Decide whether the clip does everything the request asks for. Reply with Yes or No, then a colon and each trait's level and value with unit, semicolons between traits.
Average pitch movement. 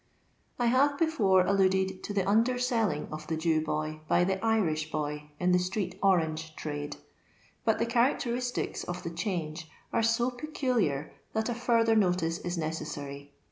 No: wide, 6.5 semitones